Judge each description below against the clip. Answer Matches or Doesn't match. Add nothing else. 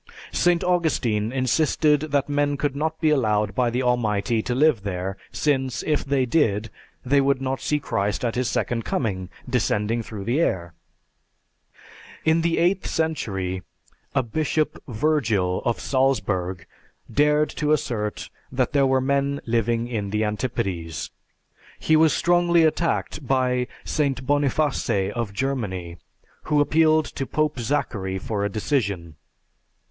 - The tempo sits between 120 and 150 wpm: Matches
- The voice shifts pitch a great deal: Matches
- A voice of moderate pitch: Doesn't match